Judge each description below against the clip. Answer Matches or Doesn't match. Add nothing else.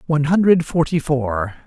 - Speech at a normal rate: Matches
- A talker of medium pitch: Matches